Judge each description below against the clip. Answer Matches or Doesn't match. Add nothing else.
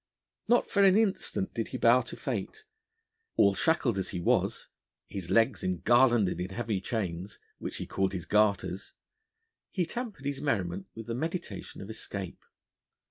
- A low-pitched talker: Matches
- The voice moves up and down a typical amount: Doesn't match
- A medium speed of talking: Matches